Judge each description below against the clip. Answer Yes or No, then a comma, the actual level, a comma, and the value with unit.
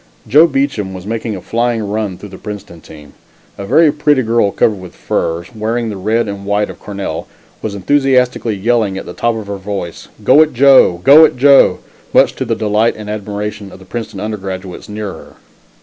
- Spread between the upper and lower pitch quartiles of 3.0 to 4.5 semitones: Yes, average, 3.3 semitones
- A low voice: Yes, low, 105 Hz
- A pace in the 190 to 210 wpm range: Yes, average, 195 wpm